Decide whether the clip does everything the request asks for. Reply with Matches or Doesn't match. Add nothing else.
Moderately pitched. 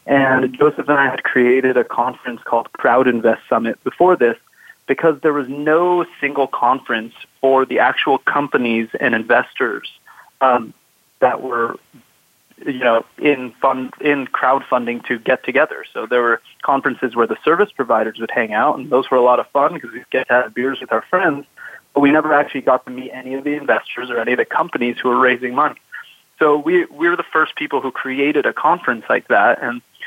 Doesn't match